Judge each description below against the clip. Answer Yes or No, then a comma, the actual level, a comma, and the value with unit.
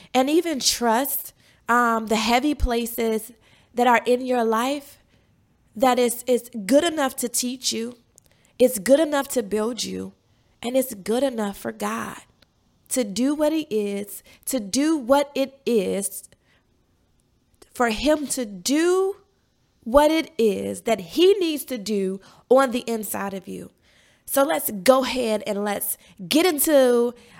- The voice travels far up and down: No, average, 3.9 semitones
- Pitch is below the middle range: No, high, 245 Hz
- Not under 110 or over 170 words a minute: Yes, average, 145 wpm